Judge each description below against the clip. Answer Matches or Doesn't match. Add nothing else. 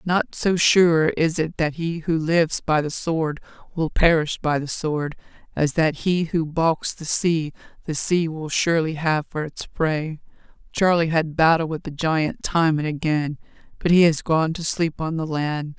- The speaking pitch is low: Doesn't match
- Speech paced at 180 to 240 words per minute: Matches